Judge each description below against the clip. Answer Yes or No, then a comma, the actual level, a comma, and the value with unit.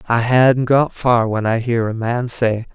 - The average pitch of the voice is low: Yes, low, 120 Hz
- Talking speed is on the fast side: Yes, fast, 220 wpm